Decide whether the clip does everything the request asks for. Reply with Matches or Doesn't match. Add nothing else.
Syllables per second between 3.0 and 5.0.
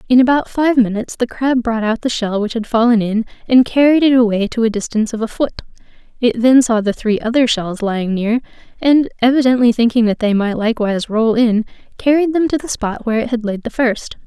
Doesn't match